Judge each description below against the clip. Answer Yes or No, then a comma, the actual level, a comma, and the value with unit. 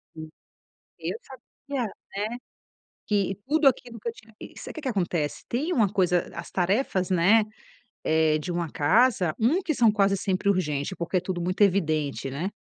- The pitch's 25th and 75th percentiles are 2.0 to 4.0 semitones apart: No, average, 5.2 semitones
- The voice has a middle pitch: No, high, 195 Hz